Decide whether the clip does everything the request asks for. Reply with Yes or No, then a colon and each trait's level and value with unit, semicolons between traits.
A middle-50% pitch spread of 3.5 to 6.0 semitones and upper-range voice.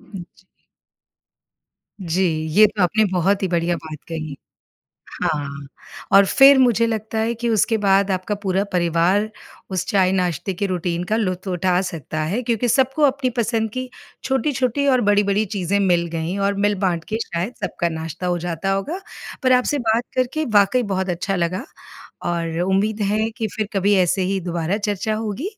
Yes: average, 4.0 semitones; high, 195 Hz